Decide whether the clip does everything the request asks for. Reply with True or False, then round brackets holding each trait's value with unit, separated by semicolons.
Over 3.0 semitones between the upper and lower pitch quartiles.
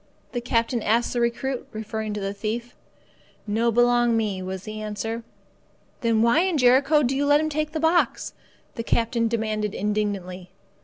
False (2.7 semitones)